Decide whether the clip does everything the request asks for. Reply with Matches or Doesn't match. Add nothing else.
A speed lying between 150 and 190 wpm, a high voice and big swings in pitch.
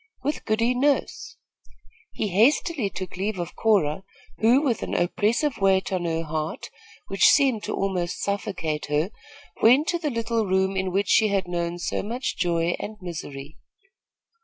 Doesn't match